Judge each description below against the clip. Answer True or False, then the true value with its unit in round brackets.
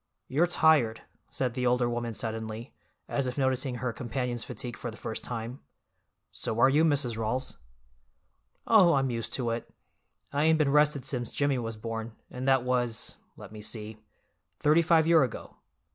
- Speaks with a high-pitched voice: False (125 Hz)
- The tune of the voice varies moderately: True (3.5 semitones)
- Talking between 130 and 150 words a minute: False (160 wpm)